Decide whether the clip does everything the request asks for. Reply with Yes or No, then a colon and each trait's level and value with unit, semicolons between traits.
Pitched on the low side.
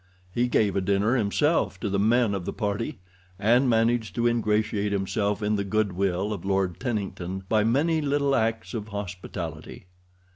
Yes: low, 105 Hz